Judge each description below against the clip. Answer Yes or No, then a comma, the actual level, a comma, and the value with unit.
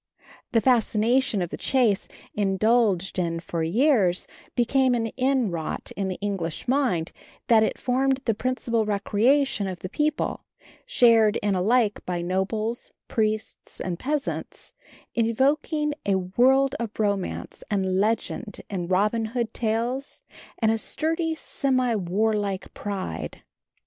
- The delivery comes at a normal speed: No, slow, 125 wpm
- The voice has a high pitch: Yes, high, 220 Hz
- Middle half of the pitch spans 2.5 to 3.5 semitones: No, average, 4.7 semitones